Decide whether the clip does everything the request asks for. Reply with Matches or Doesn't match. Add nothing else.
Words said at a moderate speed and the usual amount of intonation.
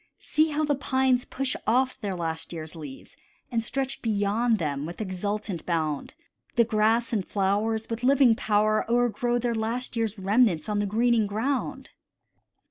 Matches